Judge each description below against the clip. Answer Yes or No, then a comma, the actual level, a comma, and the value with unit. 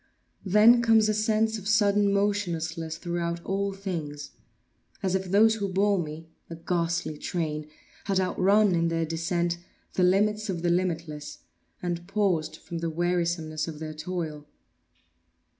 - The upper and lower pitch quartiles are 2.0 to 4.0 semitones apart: Yes, average, 3.5 semitones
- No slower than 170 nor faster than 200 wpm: No, average, 140 wpm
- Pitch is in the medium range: Yes, medium, 175 Hz